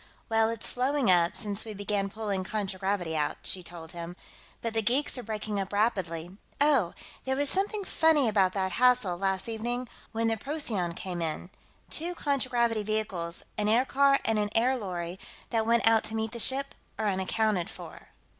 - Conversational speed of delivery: Yes, average, 175 wpm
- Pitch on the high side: Yes, high, 215 Hz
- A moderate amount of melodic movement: Yes, average, 4.4 semitones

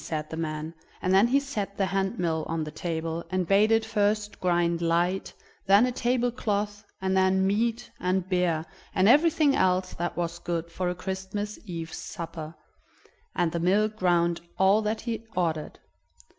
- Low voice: No, high, 190 Hz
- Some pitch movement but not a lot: Yes, average, 3.7 semitones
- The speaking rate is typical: Yes, average, 170 wpm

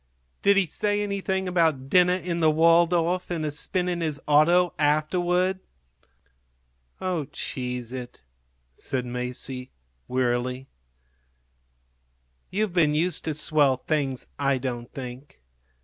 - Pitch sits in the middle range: Yes, medium, 155 Hz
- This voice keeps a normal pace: No, slow, 115 wpm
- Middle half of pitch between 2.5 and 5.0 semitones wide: No, wide, 5.4 semitones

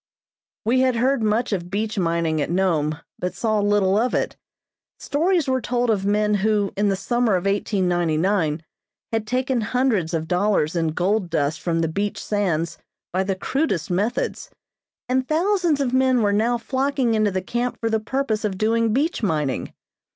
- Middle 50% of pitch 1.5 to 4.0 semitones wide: No, average, 5.2 semitones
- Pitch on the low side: No, high, 210 Hz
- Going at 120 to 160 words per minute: No, average, 175 wpm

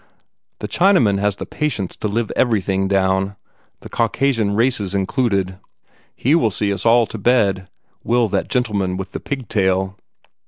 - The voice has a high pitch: No, low, 105 Hz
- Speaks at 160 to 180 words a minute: No, average, 150 wpm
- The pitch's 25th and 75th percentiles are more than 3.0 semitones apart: Yes, average, 3.6 semitones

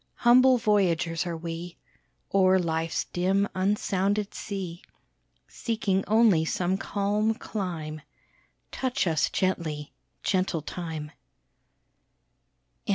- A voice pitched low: No, medium, 185 Hz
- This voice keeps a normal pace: No, slow, 90 wpm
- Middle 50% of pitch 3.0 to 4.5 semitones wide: Yes, average, 3.7 semitones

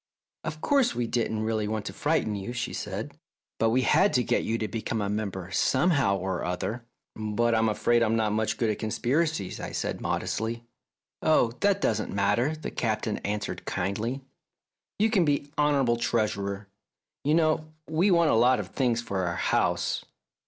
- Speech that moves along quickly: No, average, 180 wpm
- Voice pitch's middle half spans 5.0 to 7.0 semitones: Yes, average, 5.3 semitones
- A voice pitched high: No, low, 115 Hz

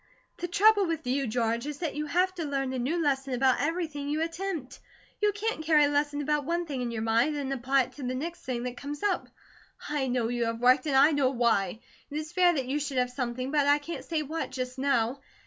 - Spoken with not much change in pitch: No, average, 3.8 semitones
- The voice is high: Yes, very high, 280 Hz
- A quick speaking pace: Yes, fast, 250 wpm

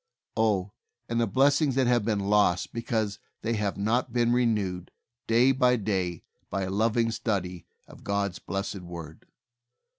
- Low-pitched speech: Yes, low, 105 Hz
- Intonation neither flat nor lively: Yes, average, 3.3 semitones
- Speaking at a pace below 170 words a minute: Yes, average, 145 wpm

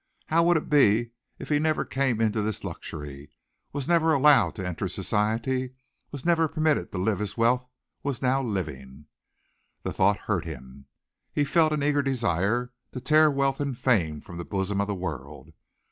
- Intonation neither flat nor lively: No, wide, 7.3 semitones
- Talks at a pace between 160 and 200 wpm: Yes, average, 175 wpm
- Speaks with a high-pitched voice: No, low, 120 Hz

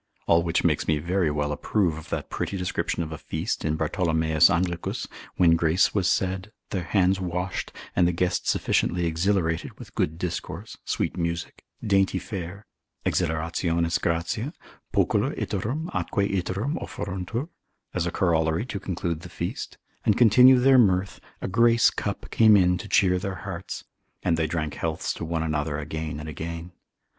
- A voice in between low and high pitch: No, very low, 90 Hz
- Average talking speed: Yes, average, 160 wpm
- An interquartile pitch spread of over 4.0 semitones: No, average, 3.0 semitones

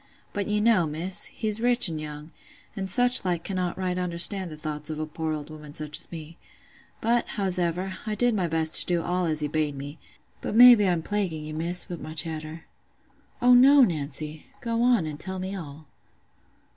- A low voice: No, medium, 175 Hz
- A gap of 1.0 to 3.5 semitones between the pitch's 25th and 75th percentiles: No, average, 4.6 semitones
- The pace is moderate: Yes, average, 195 wpm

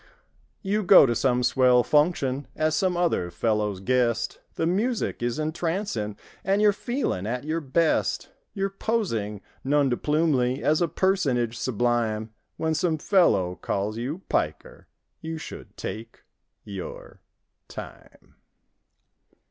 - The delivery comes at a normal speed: No, slow, 115 wpm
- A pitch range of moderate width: No, wide, 6.8 semitones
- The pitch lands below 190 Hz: Yes, medium, 140 Hz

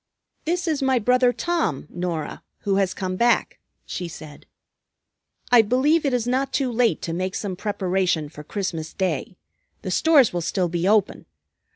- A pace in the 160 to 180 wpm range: Yes, average, 165 wpm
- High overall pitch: Yes, high, 200 Hz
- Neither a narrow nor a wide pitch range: No, wide, 6.0 semitones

